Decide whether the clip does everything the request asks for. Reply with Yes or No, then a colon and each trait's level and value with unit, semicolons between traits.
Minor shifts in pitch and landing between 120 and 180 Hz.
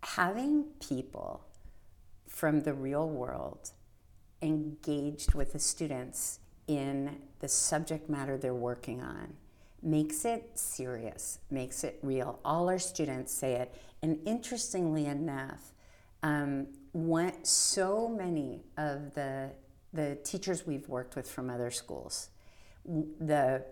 No: average, 3.6 semitones; medium, 140 Hz